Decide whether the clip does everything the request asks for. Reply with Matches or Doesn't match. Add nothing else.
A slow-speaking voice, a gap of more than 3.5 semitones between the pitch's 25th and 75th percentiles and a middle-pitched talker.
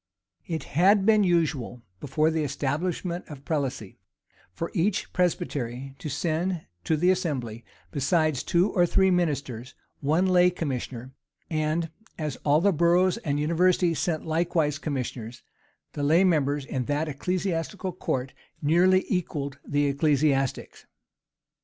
Matches